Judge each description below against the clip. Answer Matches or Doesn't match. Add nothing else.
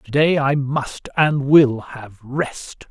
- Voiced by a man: Matches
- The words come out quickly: Doesn't match